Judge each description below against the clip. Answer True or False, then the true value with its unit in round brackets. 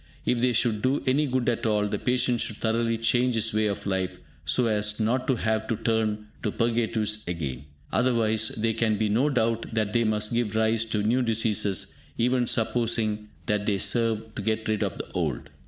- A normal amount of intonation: False (1.8 semitones)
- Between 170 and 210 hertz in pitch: False (110 Hz)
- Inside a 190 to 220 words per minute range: True (200 wpm)